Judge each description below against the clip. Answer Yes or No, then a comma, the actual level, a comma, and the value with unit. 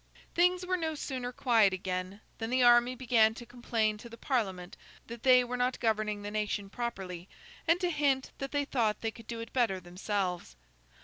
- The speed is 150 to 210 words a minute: Yes, average, 190 wpm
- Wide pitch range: No, average, 3.7 semitones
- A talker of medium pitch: No, high, 230 Hz